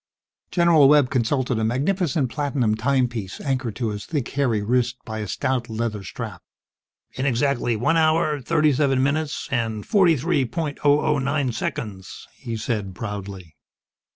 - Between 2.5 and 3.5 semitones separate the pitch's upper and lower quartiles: No, average, 4.6 semitones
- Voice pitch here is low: Yes, low, 130 Hz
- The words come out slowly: No, average, 155 wpm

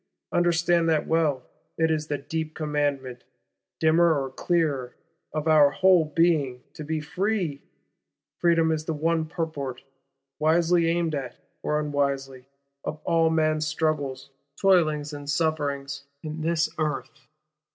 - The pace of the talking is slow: Yes, slow, 130 wpm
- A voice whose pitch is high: No, medium, 155 Hz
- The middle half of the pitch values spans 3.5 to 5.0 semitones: No, narrow, 2.4 semitones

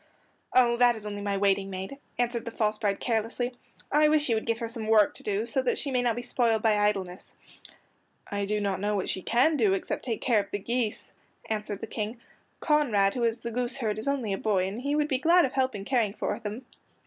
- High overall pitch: Yes, high, 225 Hz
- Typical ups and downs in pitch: Yes, average, 3.3 semitones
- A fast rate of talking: Yes, fast, 245 wpm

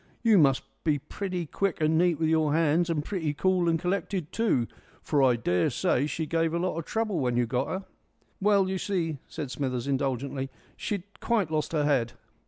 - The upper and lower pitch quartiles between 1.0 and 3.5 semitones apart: No, average, 4.7 semitones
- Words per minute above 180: Yes, average, 190 wpm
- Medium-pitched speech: Yes, medium, 160 Hz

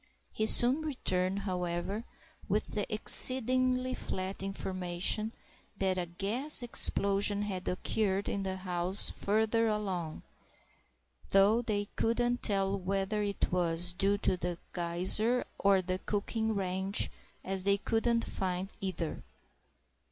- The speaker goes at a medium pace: No, slow, 120 wpm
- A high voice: Yes, high, 195 Hz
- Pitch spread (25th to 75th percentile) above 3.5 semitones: No, average, 3.0 semitones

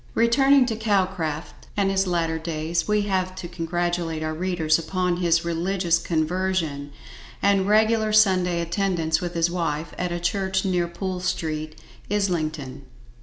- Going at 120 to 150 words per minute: Yes, average, 140 wpm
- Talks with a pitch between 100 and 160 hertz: No, medium, 175 Hz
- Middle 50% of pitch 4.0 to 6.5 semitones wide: No, average, 2.8 semitones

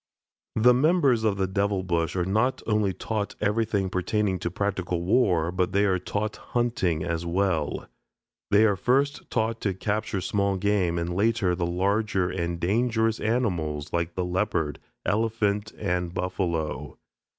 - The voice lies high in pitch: No, low, 100 Hz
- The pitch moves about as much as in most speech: Yes, average, 3.7 semitones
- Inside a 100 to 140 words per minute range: No, average, 150 wpm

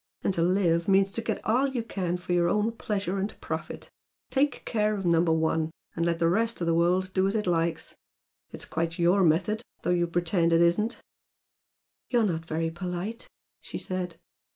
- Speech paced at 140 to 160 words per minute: No, average, 190 wpm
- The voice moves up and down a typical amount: Yes, average, 3.7 semitones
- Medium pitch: Yes, medium, 180 Hz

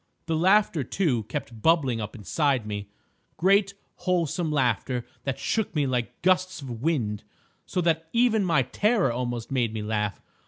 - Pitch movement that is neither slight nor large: No, wide, 7.3 semitones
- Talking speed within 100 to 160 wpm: Yes, average, 145 wpm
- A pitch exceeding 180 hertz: No, medium, 140 Hz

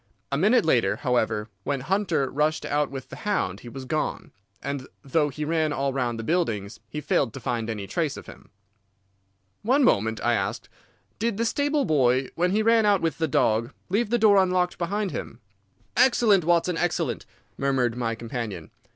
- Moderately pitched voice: Yes, medium, 150 Hz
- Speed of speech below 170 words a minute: No, average, 180 wpm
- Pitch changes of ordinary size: No, wide, 7.9 semitones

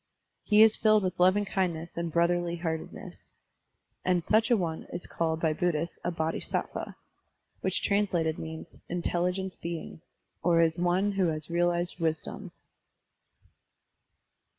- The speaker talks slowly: Yes, slow, 125 wpm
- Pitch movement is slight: Yes, narrow, 2.3 semitones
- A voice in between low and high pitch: Yes, medium, 175 Hz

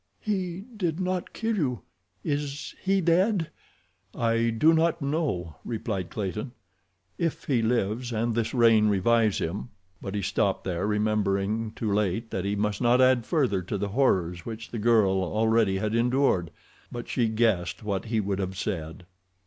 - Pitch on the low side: Yes, low, 110 Hz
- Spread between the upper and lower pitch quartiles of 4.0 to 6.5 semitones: Yes, average, 4.7 semitones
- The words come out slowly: No, average, 160 wpm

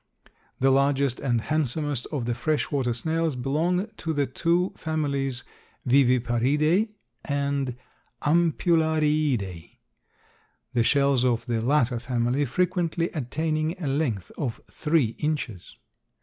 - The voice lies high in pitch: No, medium, 140 Hz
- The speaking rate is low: Yes, slow, 110 wpm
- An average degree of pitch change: Yes, average, 4.2 semitones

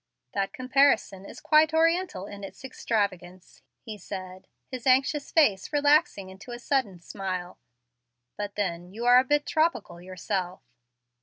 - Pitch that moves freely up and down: Yes, wide, 6.9 semitones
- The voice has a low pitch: No, high, 210 Hz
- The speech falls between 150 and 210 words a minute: No, average, 140 wpm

